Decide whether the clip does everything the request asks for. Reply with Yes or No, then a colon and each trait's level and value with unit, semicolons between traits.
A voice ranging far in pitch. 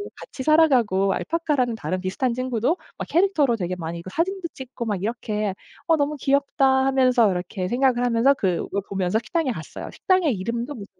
Yes: wide, 6.1 semitones